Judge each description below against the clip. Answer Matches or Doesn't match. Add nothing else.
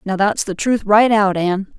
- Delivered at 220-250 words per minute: Matches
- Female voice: Matches